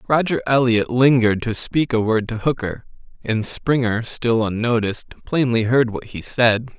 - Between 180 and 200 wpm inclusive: No, average, 160 wpm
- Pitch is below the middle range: Yes, low, 120 Hz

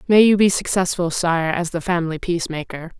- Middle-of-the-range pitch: Yes, medium, 175 Hz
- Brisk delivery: No, average, 180 wpm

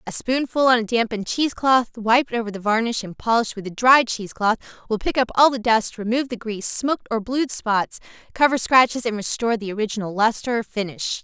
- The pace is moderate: No, fast, 215 wpm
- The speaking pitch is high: Yes, high, 230 Hz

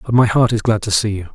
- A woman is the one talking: No, male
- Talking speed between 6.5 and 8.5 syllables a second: Yes, 6.7 syllables/s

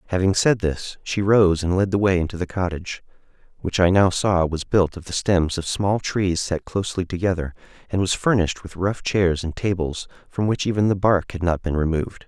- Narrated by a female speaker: No, male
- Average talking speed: No, fast, 215 wpm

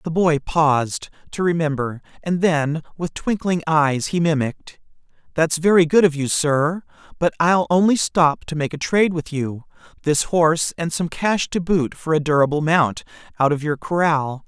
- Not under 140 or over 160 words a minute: No, average, 175 wpm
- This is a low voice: No, medium, 160 Hz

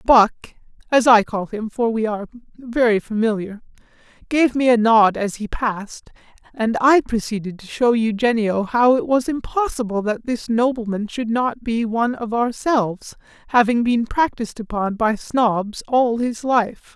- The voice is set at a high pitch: Yes, high, 230 Hz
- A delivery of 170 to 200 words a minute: No, average, 160 wpm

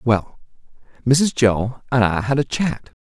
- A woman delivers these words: No, male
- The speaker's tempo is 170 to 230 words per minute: No, average, 160 wpm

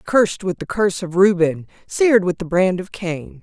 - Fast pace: Yes, fast, 210 wpm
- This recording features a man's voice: No, female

